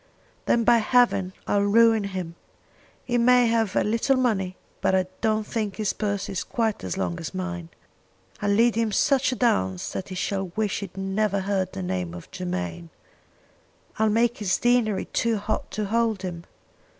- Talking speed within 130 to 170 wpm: No, average, 180 wpm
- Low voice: No, high, 205 Hz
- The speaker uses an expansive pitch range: No, average, 3.7 semitones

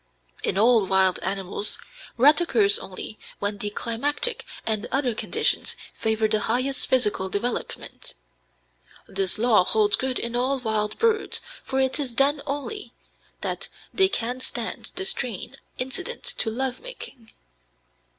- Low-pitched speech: No, high, 240 Hz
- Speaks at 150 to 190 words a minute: No, slow, 135 wpm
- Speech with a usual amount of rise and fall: Yes, average, 4.5 semitones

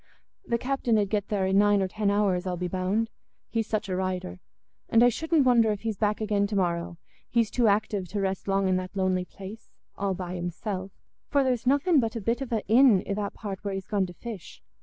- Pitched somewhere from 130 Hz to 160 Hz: No, high, 205 Hz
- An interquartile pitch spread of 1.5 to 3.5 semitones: Yes, average, 3.2 semitones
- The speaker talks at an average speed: No, fast, 230 wpm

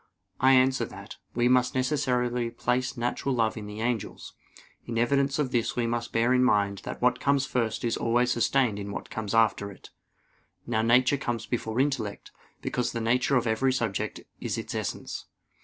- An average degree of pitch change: No, narrow, 2.1 semitones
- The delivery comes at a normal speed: Yes, average, 180 wpm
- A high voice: No, low, 120 Hz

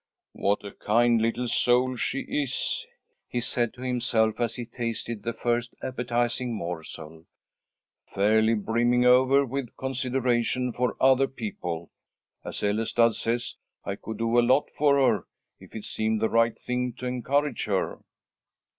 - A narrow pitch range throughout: Yes, narrow, 2.3 semitones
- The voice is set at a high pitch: No, low, 120 Hz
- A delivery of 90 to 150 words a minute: Yes, average, 145 wpm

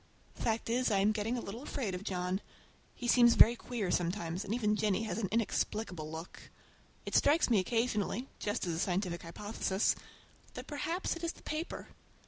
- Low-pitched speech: No, high, 215 Hz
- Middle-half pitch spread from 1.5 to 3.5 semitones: No, average, 4.4 semitones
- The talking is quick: No, average, 185 wpm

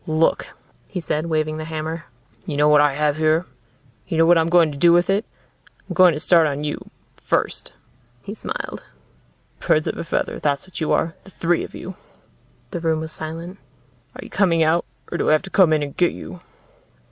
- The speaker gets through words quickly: Yes, fast, 210 wpm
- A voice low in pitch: No, medium, 160 Hz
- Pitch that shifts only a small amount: Yes, narrow, 2.0 semitones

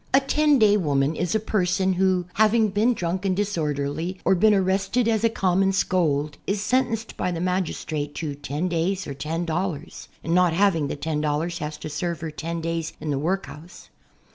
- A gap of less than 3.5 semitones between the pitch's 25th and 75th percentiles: No, average, 4.1 semitones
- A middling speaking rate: Yes, average, 195 wpm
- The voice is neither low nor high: Yes, medium, 180 Hz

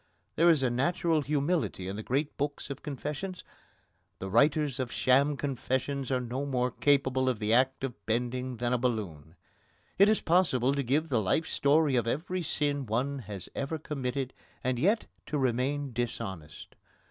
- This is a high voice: No, low, 135 Hz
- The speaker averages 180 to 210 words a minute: No, average, 170 wpm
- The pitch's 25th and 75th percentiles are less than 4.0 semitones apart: Yes, average, 3.2 semitones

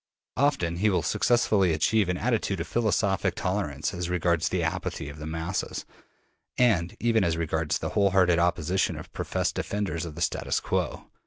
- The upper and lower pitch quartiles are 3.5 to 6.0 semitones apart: Yes, average, 3.8 semitones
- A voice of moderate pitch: No, very low, 90 Hz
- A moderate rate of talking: Yes, average, 170 wpm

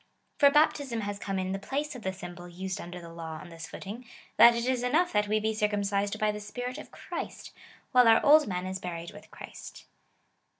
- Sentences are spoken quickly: Yes, fast, 220 wpm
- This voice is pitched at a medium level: No, high, 210 Hz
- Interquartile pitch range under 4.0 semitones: No, average, 4.9 semitones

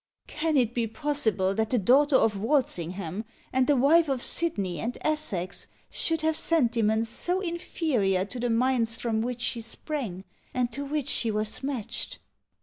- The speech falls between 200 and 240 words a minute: No, average, 160 wpm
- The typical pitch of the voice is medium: No, high, 245 Hz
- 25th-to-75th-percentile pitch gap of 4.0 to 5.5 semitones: Yes, average, 5.0 semitones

